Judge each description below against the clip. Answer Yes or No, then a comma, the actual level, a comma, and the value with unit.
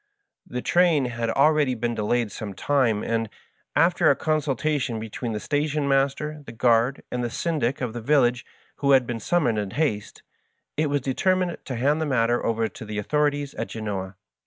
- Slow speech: No, average, 185 wpm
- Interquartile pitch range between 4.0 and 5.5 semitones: Yes, average, 4.3 semitones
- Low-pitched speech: Yes, low, 125 Hz